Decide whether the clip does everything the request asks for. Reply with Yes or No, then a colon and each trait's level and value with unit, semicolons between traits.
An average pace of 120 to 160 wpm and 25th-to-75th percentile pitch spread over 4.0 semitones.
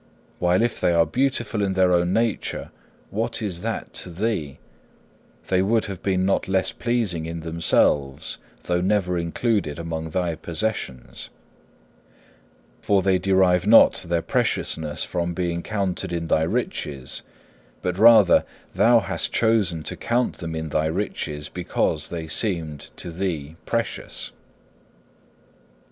No: slow, 135 wpm; average, 3.6 semitones